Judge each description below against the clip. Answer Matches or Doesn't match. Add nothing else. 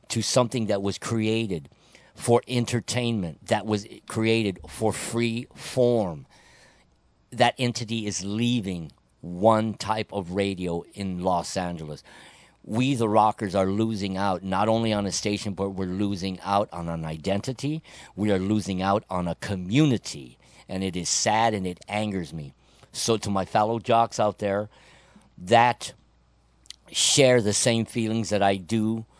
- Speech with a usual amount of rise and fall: Matches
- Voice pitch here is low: Matches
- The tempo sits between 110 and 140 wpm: Doesn't match